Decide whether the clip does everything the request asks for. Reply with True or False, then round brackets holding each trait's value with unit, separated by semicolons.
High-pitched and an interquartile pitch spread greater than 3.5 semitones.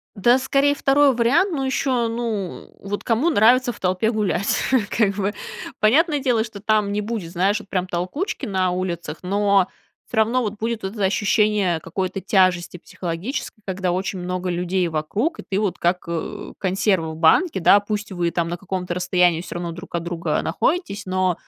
True (195 Hz; 4.0 semitones)